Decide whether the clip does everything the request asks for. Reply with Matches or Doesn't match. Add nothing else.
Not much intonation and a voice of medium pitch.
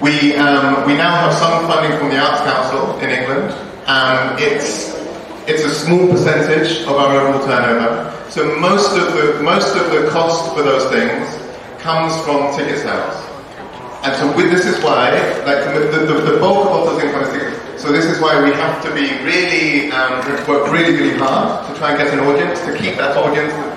Matches